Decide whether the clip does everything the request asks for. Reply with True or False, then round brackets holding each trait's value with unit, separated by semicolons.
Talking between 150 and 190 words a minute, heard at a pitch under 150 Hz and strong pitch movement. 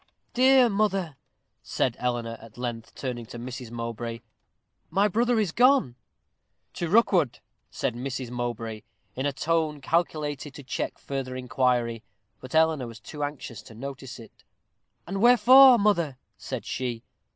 False (140 wpm; 135 Hz; 6.5 semitones)